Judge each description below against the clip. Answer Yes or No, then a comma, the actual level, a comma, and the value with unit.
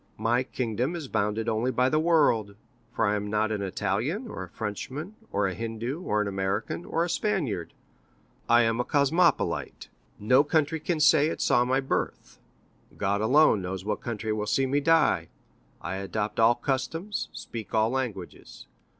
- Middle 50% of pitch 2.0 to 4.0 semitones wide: No, wide, 5.6 semitones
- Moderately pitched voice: No, low, 115 Hz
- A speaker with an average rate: Yes, average, 165 wpm